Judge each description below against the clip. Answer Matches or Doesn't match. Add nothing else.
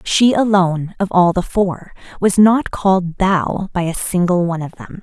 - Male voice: Doesn't match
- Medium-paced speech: Matches